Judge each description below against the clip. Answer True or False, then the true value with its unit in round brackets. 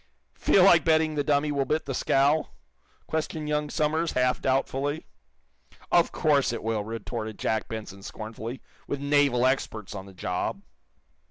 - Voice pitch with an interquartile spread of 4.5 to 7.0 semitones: True (5.1 semitones)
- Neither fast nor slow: True (150 wpm)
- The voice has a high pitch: False (135 Hz)